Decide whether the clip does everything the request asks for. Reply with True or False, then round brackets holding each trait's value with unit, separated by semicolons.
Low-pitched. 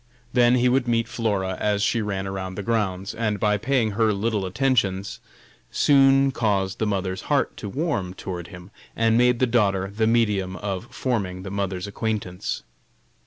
True (105 Hz)